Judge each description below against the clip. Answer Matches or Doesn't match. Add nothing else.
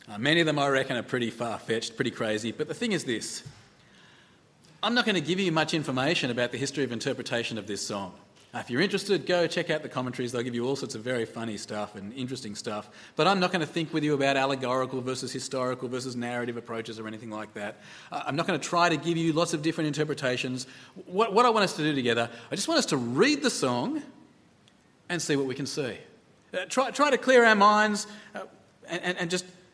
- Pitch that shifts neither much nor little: Doesn't match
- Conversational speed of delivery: Doesn't match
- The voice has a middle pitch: Matches